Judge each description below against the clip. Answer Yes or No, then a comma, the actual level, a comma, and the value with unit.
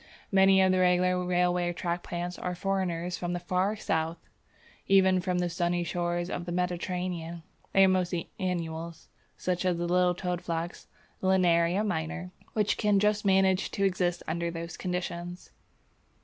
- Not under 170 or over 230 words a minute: No, average, 150 wpm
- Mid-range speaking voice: Yes, medium, 180 Hz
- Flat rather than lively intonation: Yes, narrow, 1.3 semitones